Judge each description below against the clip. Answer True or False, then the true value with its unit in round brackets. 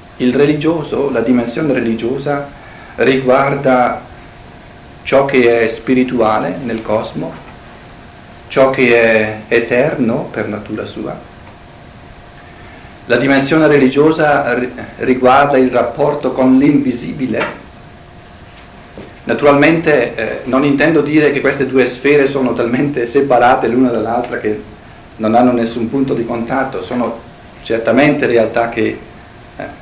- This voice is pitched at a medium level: False (130 Hz)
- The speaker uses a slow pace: True (105 wpm)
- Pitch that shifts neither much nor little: True (3.2 semitones)